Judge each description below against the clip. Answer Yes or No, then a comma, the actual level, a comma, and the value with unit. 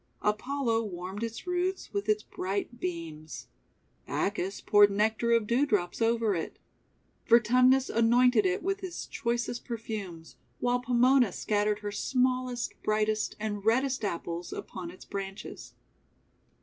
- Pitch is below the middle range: No, high, 220 Hz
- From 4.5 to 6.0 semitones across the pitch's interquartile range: No, average, 3.7 semitones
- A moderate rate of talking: No, slow, 125 wpm